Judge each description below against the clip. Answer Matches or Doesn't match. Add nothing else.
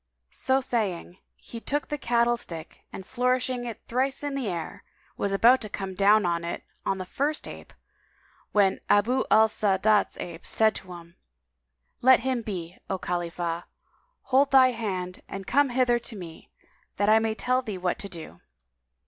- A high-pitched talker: Matches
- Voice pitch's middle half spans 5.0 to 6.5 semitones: Matches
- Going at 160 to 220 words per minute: Matches